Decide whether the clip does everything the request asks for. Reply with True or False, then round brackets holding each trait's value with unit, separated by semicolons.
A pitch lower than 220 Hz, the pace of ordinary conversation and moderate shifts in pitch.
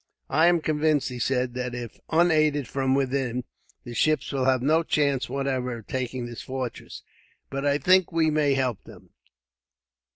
True (135 Hz; 170 wpm; 3.3 semitones)